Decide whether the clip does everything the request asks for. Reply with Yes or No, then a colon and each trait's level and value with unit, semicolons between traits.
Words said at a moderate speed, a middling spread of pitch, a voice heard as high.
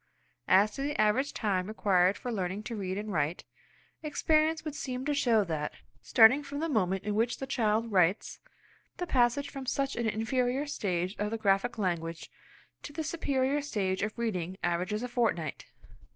No: average, 175 wpm; wide, 6.0 semitones; high, 220 Hz